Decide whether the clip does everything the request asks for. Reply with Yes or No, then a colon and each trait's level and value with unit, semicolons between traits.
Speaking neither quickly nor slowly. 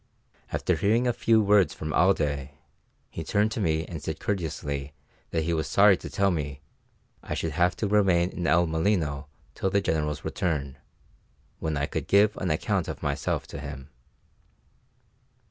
Yes: average, 165 wpm